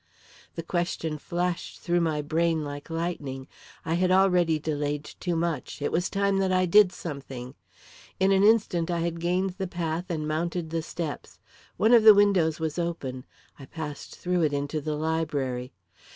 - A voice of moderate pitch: Yes, medium, 165 Hz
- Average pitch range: Yes, average, 3.0 semitones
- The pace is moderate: Yes, average, 170 wpm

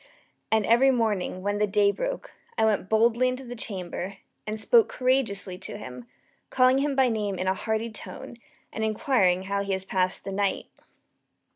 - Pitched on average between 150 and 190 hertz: No, high, 215 Hz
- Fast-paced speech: No, average, 175 wpm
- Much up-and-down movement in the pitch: No, average, 4.4 semitones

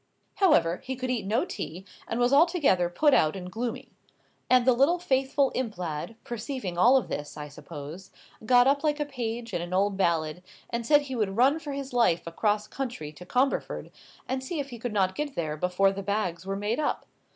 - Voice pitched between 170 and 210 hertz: No, high, 230 Hz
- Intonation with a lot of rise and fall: Yes, wide, 6.7 semitones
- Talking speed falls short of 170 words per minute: No, fast, 205 wpm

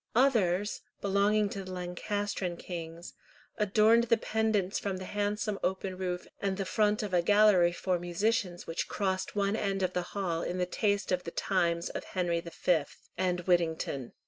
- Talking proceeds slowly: No, average, 170 wpm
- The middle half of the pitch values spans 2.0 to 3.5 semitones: Yes, average, 2.7 semitones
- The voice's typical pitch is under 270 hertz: Yes, high, 190 Hz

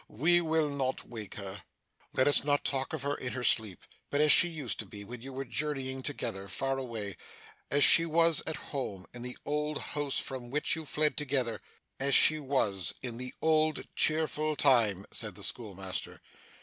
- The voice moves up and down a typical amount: Yes, average, 4.4 semitones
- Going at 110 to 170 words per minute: No, average, 190 wpm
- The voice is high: No, low, 135 Hz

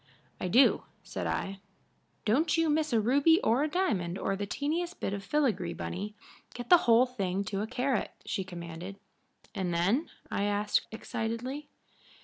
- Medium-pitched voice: No, high, 225 Hz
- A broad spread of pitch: Yes, wide, 6.5 semitones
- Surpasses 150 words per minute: Yes, average, 160 wpm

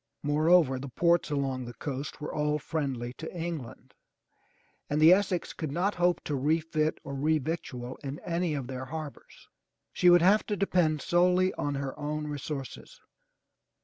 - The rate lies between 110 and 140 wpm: No, average, 160 wpm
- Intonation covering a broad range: No, average, 3.8 semitones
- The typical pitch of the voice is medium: Yes, medium, 150 Hz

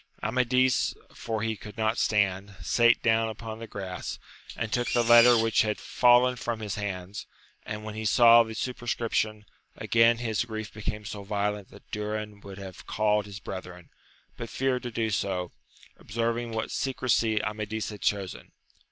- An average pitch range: No, narrow, 2.2 semitones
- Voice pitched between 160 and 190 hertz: No, low, 110 Hz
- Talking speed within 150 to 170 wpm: Yes, average, 160 wpm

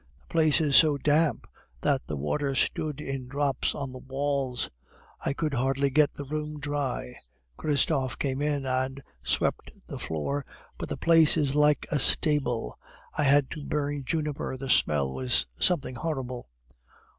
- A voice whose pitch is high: No, medium, 140 Hz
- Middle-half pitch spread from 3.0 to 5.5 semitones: No, narrow, 2.4 semitones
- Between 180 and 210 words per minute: No, average, 155 wpm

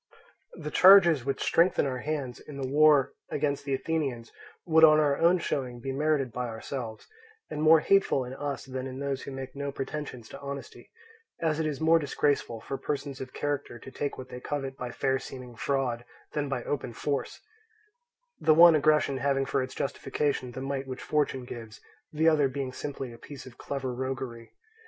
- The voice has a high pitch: No, medium, 140 Hz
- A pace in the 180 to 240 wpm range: Yes, average, 190 wpm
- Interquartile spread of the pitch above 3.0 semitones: No, narrow, 2.5 semitones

